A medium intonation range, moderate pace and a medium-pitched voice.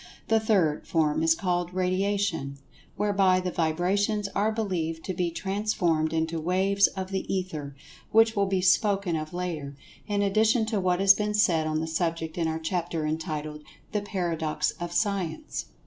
Yes: average, 3.8 semitones; average, 165 wpm; medium, 180 Hz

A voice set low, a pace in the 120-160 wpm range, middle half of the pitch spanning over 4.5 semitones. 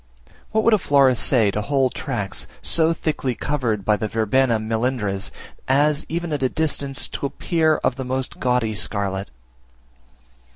Yes: low, 130 Hz; average, 155 wpm; average, 5.0 semitones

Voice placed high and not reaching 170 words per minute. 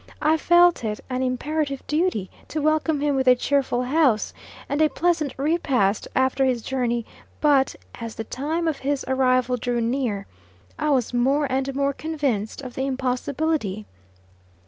Yes: very high, 265 Hz; average, 155 wpm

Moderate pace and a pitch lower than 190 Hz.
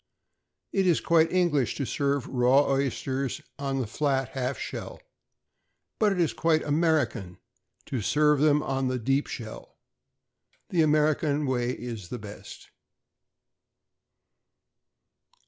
No: slow, 120 wpm; medium, 140 Hz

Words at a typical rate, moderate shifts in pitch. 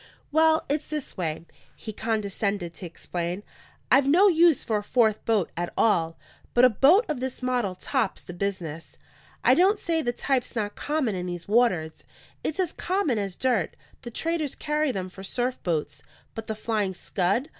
No: average, 175 wpm; wide, 7.4 semitones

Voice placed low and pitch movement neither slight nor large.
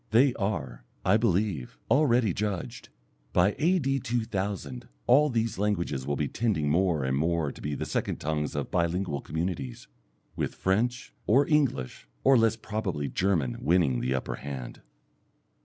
No: very low, 95 Hz; wide, 7.5 semitones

